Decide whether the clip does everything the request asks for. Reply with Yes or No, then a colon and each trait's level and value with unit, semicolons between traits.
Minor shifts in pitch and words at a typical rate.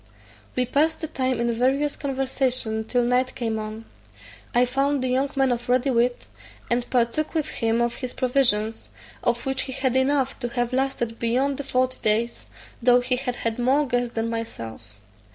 Yes: narrow, 2.2 semitones; average, 180 wpm